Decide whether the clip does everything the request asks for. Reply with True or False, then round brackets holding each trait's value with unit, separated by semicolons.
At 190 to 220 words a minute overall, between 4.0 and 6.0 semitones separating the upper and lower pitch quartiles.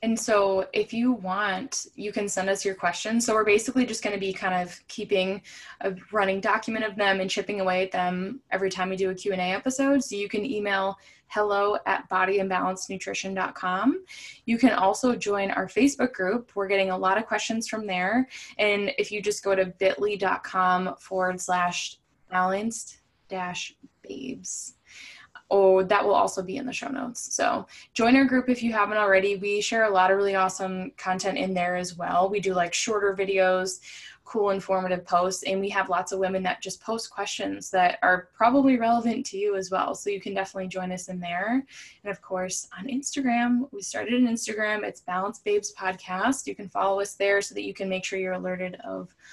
False (200 wpm; 3.0 semitones)